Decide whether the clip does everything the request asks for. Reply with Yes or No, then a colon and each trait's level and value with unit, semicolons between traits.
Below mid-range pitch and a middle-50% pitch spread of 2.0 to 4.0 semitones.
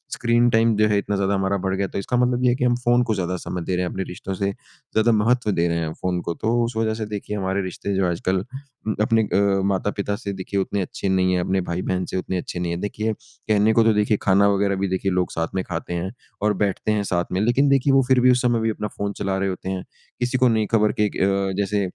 Yes: low, 100 Hz; average, 2.8 semitones